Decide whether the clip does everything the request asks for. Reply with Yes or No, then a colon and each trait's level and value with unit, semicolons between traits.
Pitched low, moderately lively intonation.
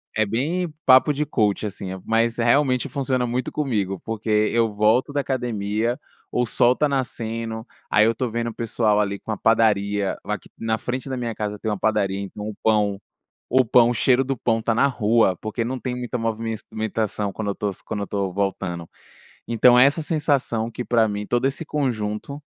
Yes: low, 115 Hz; average, 3.2 semitones